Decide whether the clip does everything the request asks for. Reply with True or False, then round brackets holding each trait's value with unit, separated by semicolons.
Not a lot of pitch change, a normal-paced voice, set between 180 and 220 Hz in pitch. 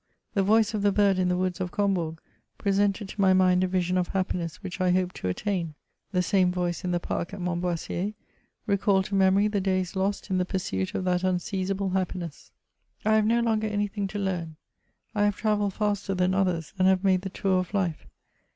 False (1.8 semitones; 210 wpm; 190 Hz)